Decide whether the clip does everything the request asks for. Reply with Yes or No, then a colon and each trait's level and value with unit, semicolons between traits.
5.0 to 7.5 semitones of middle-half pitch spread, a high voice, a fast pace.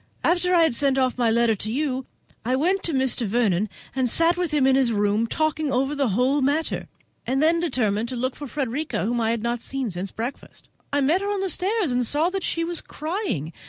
Yes: average, 5.3 semitones; very high, 265 Hz; fast, 230 wpm